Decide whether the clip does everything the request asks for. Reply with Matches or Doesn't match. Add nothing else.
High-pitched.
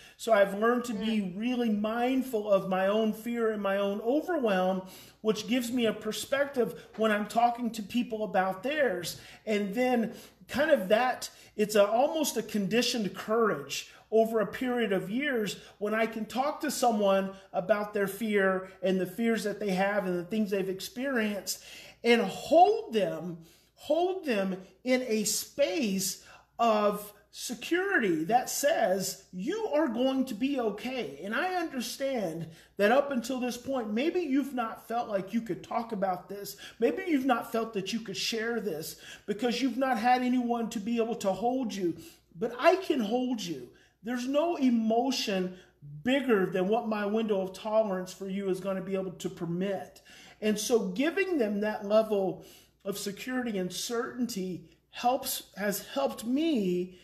Matches